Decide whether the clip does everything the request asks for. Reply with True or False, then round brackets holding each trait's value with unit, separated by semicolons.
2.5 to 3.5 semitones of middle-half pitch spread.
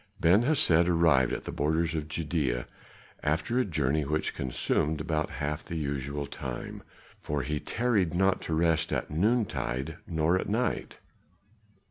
True (3.0 semitones)